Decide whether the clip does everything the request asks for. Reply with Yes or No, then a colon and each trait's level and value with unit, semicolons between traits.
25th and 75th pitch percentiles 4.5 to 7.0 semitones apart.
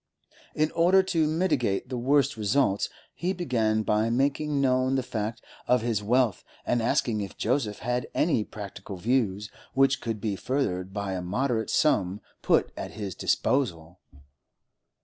Yes: average, 4.9 semitones